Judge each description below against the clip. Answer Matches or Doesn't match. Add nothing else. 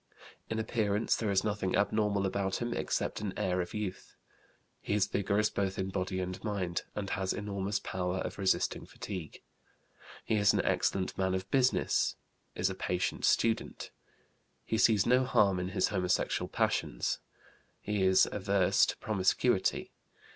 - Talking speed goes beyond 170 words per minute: Doesn't match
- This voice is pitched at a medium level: Doesn't match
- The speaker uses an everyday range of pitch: Doesn't match